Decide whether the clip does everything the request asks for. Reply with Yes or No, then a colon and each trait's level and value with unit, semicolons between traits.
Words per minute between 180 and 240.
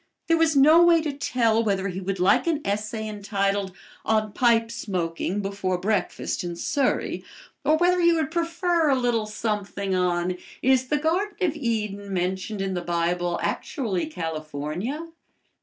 No: average, 155 wpm